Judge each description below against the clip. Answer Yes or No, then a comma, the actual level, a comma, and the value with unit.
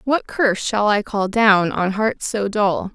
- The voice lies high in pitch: Yes, high, 210 Hz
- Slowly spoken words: No, fast, 205 wpm